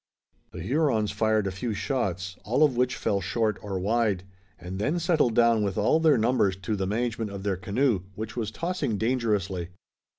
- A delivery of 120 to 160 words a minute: No, average, 185 wpm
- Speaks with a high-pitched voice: No, low, 110 Hz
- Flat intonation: No, average, 4.0 semitones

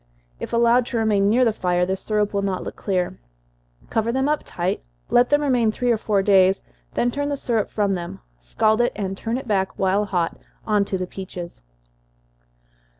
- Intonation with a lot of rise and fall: No, average, 3.7 semitones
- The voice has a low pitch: No, high, 210 Hz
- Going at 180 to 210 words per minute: Yes, average, 195 wpm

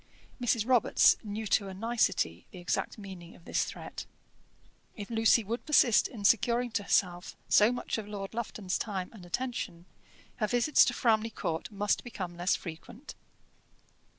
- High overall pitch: Yes, high, 210 Hz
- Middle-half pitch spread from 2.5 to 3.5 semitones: No, average, 3.9 semitones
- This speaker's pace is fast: No, average, 155 wpm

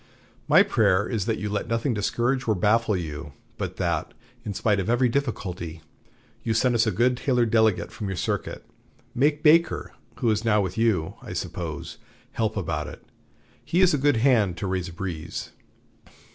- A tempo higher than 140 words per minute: Yes, average, 180 wpm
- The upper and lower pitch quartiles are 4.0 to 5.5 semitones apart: Yes, average, 4.7 semitones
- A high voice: No, low, 110 Hz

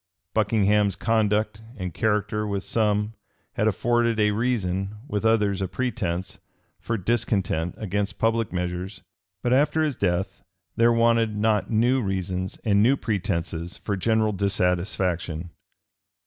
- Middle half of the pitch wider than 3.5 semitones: No, average, 3.1 semitones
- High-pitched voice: No, low, 105 Hz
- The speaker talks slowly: Yes, slow, 125 wpm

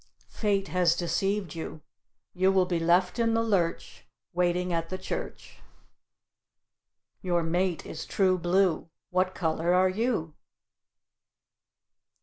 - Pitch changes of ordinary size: No, narrow, 2.0 semitones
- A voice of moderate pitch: Yes, medium, 180 Hz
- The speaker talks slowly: Yes, slow, 120 wpm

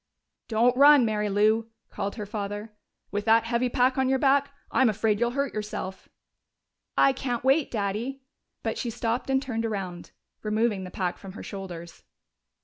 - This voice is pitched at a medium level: No, high, 225 Hz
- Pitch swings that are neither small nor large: Yes, average, 3.7 semitones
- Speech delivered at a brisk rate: No, average, 165 wpm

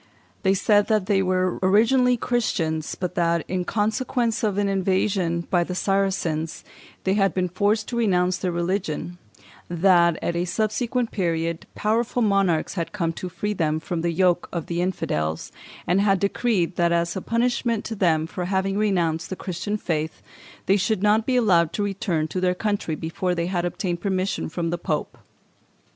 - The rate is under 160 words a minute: No, average, 175 wpm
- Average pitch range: Yes, average, 3.3 semitones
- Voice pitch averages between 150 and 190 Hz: Yes, medium, 185 Hz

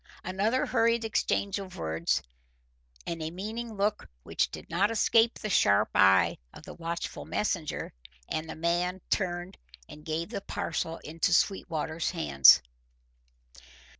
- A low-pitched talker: No, medium, 175 Hz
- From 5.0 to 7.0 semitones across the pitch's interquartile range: No, average, 4.6 semitones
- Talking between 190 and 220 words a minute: No, slow, 135 wpm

